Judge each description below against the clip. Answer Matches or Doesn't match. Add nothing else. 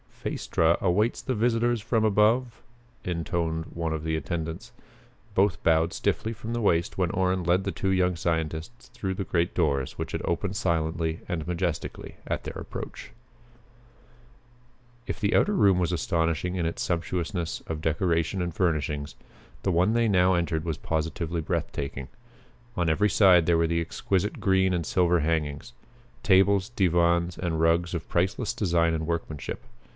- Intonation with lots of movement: Doesn't match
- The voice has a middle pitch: Doesn't match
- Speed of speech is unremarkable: Matches